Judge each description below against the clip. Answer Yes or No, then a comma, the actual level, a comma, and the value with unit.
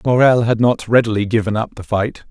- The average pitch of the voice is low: Yes, low, 110 Hz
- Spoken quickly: Yes, fast, 235 wpm